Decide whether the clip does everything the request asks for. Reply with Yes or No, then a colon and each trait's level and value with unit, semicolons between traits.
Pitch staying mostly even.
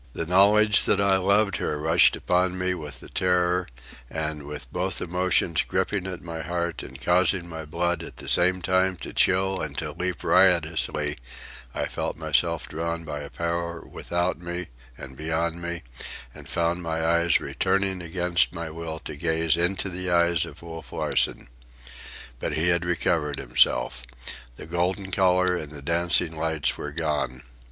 Yes: narrow, 2.2 semitones